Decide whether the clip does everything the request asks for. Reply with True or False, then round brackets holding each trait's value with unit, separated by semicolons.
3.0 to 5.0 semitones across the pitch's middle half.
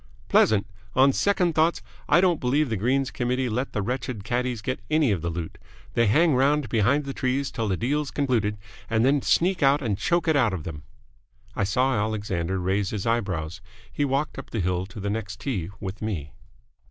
False (5.5 semitones)